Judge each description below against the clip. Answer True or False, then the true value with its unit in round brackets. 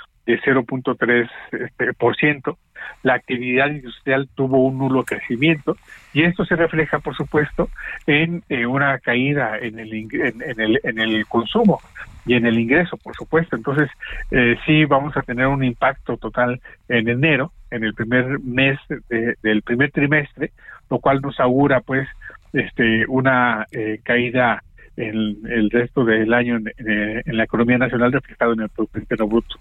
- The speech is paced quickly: False (165 wpm)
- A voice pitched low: True (125 Hz)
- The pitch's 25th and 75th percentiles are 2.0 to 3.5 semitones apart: True (3.2 semitones)